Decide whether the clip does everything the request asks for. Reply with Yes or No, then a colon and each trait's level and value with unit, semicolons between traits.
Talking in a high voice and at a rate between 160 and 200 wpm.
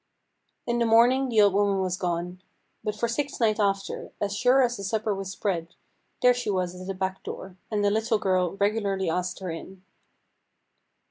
Yes: high, 200 Hz; average, 190 wpm